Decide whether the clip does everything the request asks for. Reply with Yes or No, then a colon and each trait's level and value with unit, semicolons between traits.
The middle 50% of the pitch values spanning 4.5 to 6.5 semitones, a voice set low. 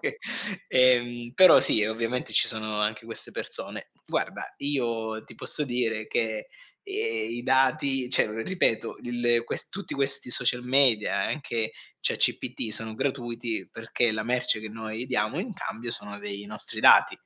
No: narrow, 2.5 semitones; low, 120 Hz